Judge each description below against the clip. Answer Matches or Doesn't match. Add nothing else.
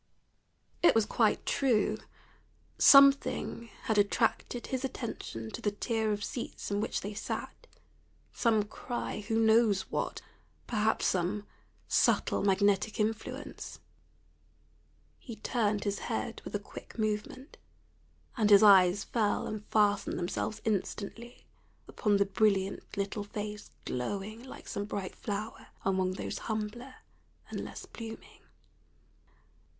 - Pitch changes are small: Matches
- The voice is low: Doesn't match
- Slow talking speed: Matches